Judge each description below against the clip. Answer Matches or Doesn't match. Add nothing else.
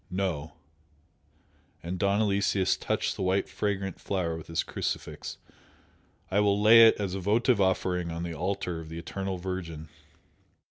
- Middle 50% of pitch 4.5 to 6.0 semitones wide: Doesn't match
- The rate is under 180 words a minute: Matches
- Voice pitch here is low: Matches